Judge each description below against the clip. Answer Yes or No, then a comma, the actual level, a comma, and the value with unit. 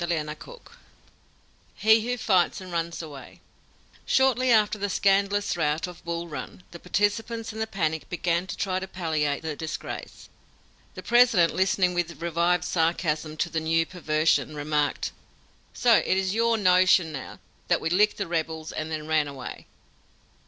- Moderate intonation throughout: Yes, average, 4.0 semitones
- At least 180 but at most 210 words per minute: No, average, 155 wpm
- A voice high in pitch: No, medium, 175 Hz